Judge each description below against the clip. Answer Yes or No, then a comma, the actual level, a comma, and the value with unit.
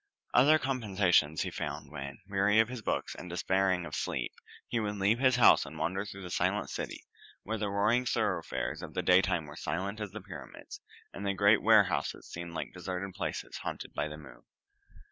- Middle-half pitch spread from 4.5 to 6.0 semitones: No, average, 3.6 semitones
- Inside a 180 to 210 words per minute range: Yes, average, 190 wpm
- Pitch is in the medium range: No, low, 100 Hz